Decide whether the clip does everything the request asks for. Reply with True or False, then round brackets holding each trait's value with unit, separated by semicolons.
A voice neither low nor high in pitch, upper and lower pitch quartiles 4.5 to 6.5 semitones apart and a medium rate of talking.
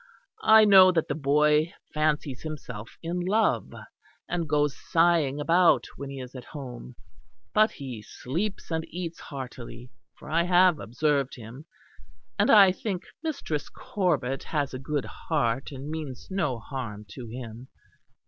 True (150 Hz; 5.1 semitones; 145 wpm)